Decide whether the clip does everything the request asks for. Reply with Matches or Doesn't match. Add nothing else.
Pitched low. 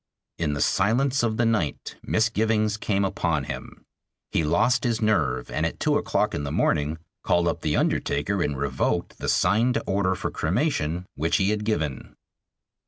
Matches